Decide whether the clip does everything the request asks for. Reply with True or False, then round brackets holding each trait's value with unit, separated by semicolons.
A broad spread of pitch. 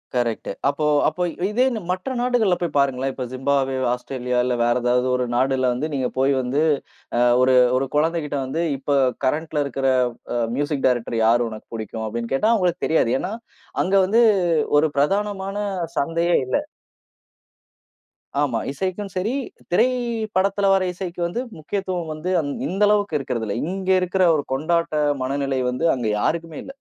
True (6.3 semitones)